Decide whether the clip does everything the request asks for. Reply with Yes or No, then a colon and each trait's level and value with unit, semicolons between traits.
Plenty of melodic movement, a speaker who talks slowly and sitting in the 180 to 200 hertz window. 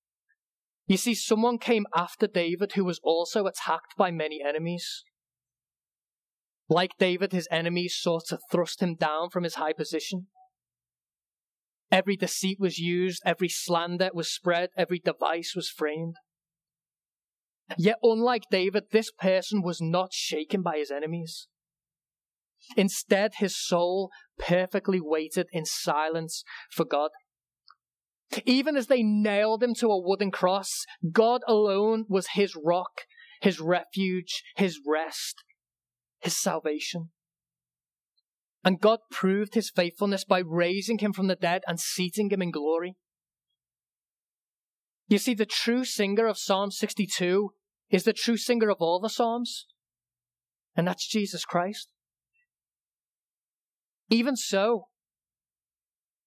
No: average, 3.9 semitones; slow, 125 wpm; medium, 185 Hz